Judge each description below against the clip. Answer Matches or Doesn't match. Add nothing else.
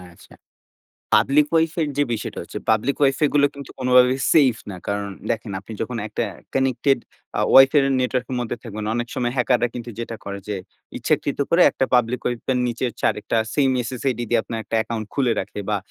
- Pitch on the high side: Doesn't match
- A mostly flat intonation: Doesn't match